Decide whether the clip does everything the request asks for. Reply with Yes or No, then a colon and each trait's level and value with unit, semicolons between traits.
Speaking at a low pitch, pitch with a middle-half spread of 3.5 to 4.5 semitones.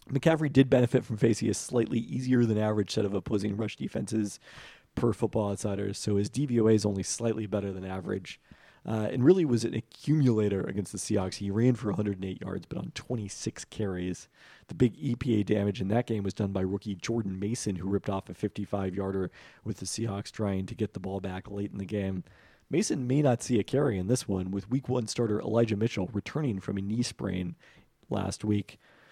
No: low, 105 Hz; average, 3.1 semitones